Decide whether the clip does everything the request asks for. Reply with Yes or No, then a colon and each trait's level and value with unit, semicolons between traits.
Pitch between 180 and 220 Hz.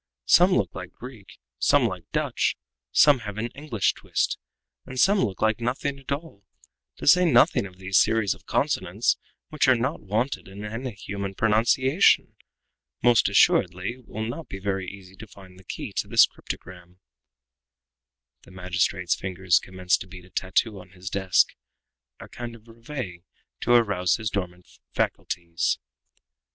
No: low, 105 Hz